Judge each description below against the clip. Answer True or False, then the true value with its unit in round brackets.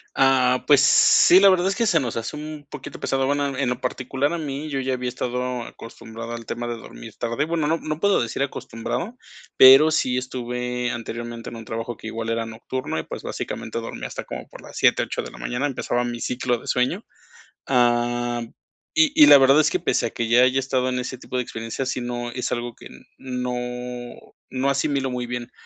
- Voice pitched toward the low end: True (125 Hz)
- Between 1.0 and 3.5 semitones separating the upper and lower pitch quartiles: True (2.7 semitones)